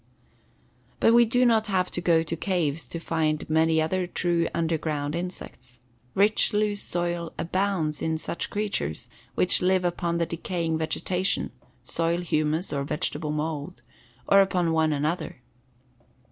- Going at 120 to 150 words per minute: Yes, average, 140 wpm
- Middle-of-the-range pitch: Yes, medium, 170 Hz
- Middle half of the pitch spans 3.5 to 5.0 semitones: No, narrow, 2.6 semitones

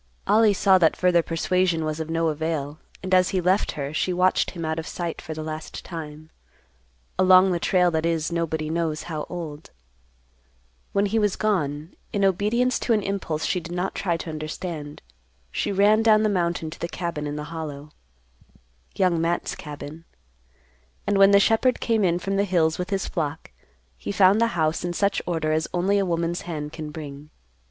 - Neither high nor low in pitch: Yes, medium, 170 Hz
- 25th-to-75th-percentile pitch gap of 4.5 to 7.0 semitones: No, average, 3.4 semitones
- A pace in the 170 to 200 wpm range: Yes, average, 185 wpm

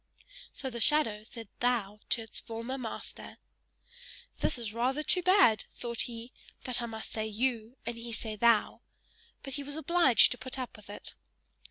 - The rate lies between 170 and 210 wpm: Yes, average, 180 wpm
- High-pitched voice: Yes, high, 235 Hz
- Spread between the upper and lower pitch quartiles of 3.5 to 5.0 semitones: No, average, 2.8 semitones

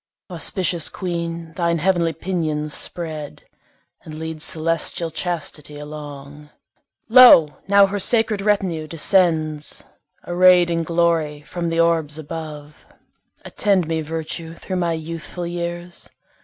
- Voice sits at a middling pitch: Yes, medium, 165 Hz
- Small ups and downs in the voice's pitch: Yes, narrow, 2.2 semitones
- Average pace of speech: No, slow, 115 wpm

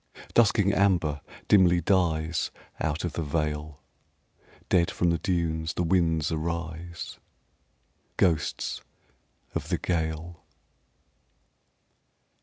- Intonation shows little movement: Yes, narrow, 1.8 semitones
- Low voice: Yes, very low, 85 Hz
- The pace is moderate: No, slow, 90 wpm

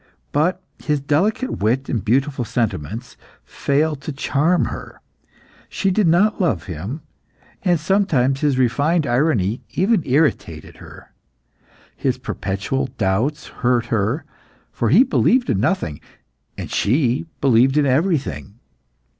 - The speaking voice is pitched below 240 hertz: Yes, low, 135 Hz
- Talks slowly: Yes, slow, 120 wpm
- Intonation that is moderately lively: No, wide, 5.7 semitones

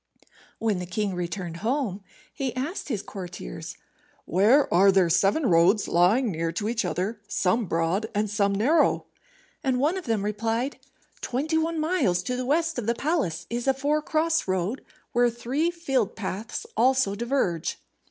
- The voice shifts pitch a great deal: Yes, wide, 6.2 semitones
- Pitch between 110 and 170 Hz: No, high, 225 Hz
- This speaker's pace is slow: No, average, 160 wpm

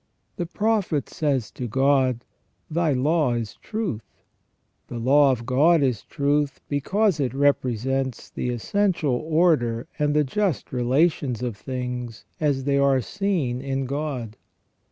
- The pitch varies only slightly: No, average, 3.8 semitones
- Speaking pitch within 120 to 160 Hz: Yes, low, 135 Hz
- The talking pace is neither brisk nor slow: Yes, average, 145 wpm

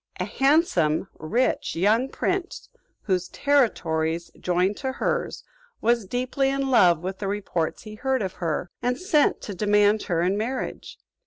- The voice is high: Yes, high, 210 Hz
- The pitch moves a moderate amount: No, wide, 6.6 semitones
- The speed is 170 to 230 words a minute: No, average, 150 wpm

